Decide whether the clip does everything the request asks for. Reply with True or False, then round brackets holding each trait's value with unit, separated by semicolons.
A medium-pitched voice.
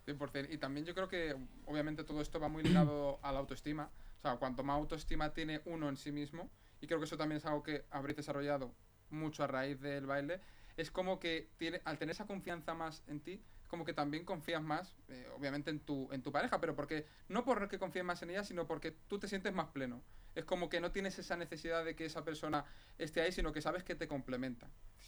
True (155 Hz)